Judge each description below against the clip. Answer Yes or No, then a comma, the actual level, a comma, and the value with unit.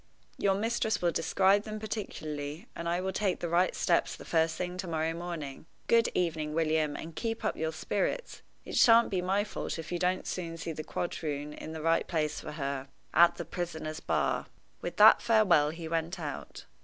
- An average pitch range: Yes, average, 3.2 semitones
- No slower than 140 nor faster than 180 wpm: No, average, 195 wpm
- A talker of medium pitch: Yes, medium, 170 Hz